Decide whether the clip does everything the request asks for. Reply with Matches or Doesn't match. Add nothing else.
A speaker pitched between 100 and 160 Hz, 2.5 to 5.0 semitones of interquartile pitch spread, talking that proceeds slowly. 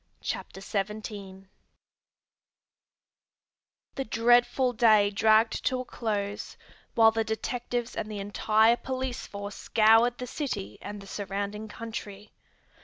Doesn't match